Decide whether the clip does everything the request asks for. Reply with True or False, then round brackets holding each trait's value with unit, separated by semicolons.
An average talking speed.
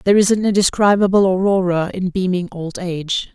True (160 wpm)